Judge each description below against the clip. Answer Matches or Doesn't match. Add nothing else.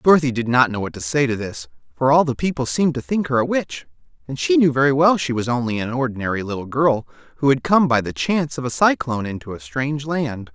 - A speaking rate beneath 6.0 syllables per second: Doesn't match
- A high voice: Doesn't match